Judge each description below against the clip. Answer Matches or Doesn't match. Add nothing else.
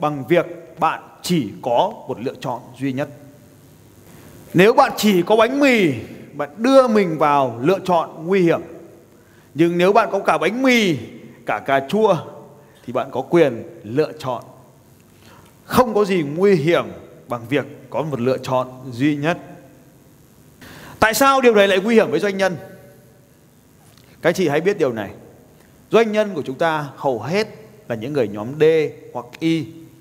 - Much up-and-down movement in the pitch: Matches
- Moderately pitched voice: Matches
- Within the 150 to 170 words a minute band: Matches